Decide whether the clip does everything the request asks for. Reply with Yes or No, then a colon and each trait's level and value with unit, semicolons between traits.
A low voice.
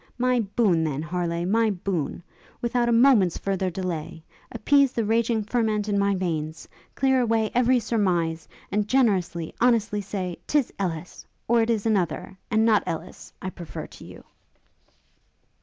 No: high, 205 Hz